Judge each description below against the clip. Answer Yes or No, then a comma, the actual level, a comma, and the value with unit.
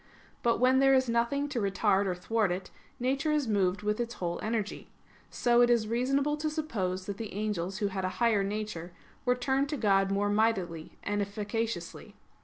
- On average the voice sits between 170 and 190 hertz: No, high, 215 Hz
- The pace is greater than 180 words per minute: Yes, average, 190 wpm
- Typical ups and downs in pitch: Yes, average, 4.0 semitones